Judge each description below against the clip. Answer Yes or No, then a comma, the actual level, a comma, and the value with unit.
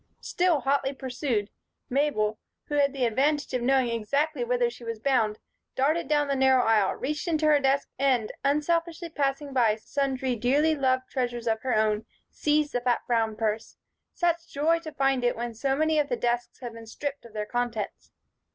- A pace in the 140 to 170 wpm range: No, average, 185 wpm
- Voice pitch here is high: Yes, very high, 265 Hz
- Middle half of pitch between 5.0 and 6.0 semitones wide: No, average, 3.7 semitones